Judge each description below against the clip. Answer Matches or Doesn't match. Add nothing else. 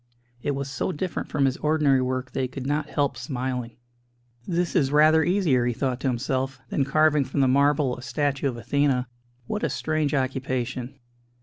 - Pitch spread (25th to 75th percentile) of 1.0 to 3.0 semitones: Matches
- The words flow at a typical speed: Matches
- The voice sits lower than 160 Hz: Matches